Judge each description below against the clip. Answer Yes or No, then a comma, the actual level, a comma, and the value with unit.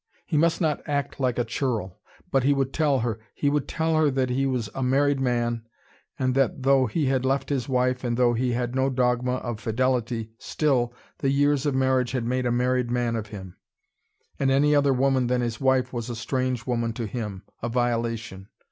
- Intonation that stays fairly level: Yes, narrow, 2.3 semitones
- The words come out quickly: Yes, fast, 210 wpm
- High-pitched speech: No, low, 125 Hz